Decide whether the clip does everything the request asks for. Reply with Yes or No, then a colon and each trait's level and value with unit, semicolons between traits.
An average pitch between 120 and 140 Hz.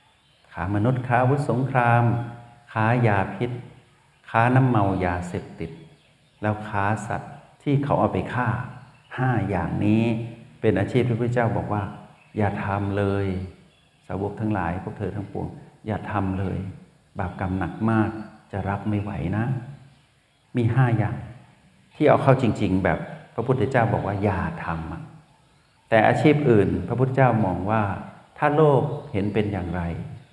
No: low, 110 Hz